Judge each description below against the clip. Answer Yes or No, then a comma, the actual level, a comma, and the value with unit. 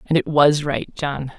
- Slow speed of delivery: No, fast, 215 wpm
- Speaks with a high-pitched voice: No, medium, 145 Hz